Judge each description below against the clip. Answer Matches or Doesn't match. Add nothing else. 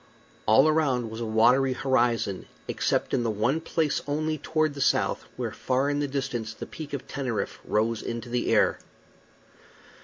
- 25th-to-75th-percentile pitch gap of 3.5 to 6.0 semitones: Matches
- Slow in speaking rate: Doesn't match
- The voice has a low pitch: Matches